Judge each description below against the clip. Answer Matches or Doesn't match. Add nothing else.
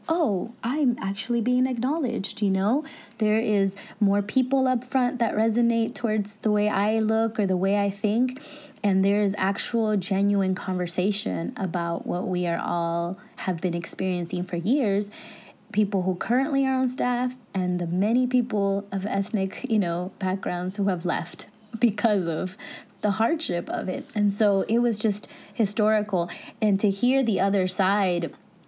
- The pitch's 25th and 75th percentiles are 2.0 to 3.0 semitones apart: Doesn't match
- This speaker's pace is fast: Doesn't match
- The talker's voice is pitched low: Doesn't match